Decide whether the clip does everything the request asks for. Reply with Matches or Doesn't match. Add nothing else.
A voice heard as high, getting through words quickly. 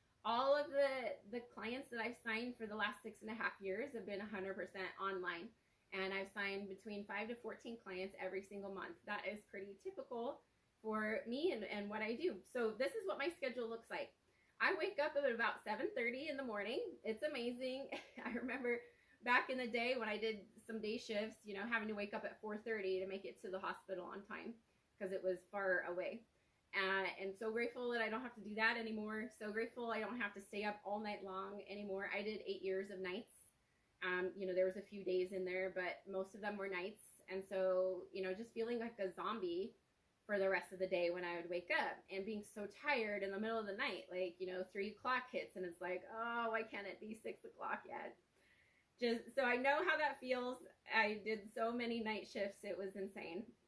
Matches